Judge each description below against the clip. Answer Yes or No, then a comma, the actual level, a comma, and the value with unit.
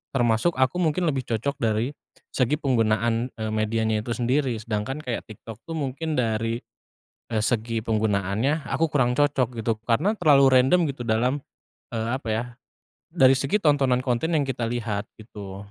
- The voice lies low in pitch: Yes, low, 120 Hz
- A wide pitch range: No, average, 3.7 semitones